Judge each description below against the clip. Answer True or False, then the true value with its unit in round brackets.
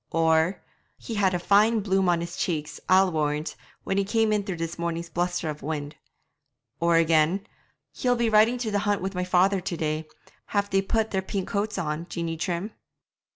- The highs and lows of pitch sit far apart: False (3.6 semitones)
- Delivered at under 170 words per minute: False (195 wpm)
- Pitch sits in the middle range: True (180 Hz)